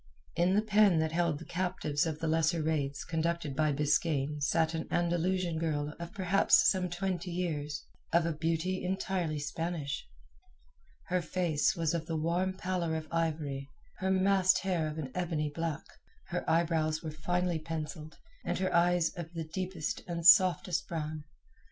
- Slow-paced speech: No, average, 160 wpm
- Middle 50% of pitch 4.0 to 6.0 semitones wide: No, narrow, 2.5 semitones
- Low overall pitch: No, medium, 165 Hz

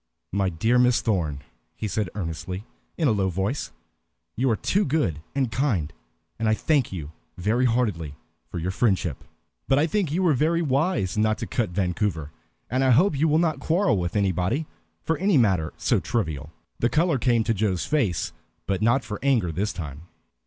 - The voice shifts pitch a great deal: Yes, wide, 7.2 semitones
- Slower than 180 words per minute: No, average, 185 wpm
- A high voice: No, low, 110 Hz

